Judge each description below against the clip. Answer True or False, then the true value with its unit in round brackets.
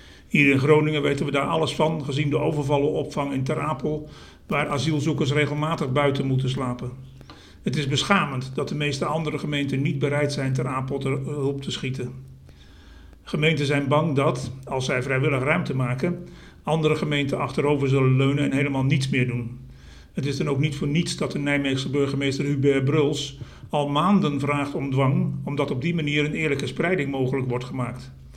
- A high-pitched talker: False (140 Hz)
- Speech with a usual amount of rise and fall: False (2.1 semitones)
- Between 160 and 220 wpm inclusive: True (180 wpm)